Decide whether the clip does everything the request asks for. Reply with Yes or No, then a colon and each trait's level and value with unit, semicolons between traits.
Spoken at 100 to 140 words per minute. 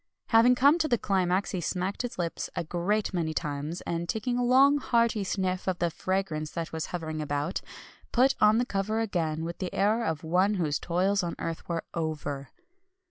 No: average, 190 wpm